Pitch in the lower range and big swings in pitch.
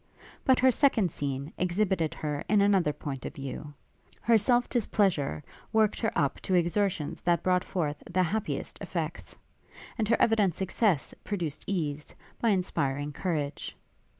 No: medium, 180 Hz; wide, 6.0 semitones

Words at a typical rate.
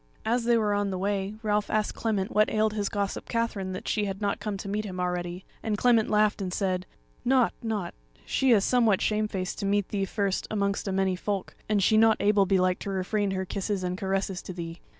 No: fast, 220 wpm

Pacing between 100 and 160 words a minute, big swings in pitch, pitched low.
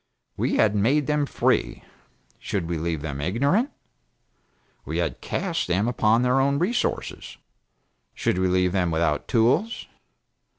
Yes: slow, 135 wpm; wide, 8.1 semitones; low, 110 Hz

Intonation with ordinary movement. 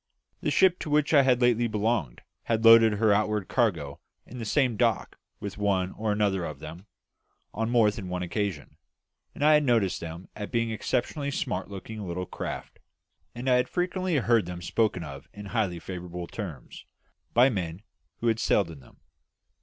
Yes: average, 4.8 semitones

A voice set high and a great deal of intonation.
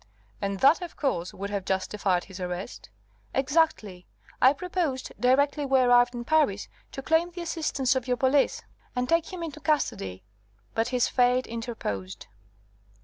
Yes: very high, 255 Hz; wide, 6.7 semitones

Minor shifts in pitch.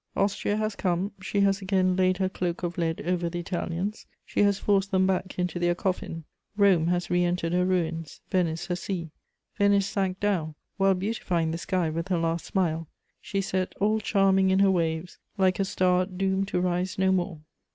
Yes: narrow, 1.9 semitones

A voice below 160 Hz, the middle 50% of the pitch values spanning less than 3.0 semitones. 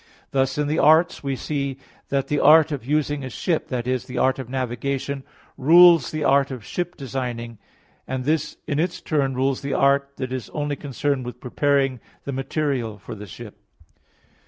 Yes: medium, 140 Hz; narrow, 2.4 semitones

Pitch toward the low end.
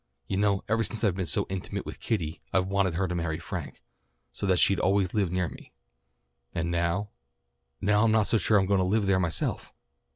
Yes: very low, 95 Hz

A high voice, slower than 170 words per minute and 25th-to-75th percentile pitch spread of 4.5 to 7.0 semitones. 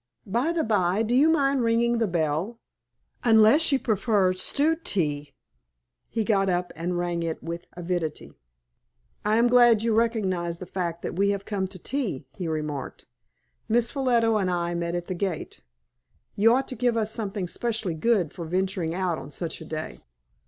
No: high, 195 Hz; average, 175 wpm; average, 5.1 semitones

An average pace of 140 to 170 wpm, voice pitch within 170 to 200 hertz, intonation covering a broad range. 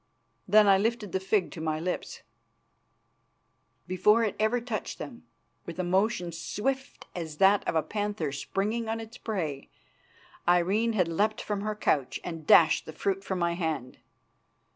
No: average, 160 wpm; high, 190 Hz; average, 4.3 semitones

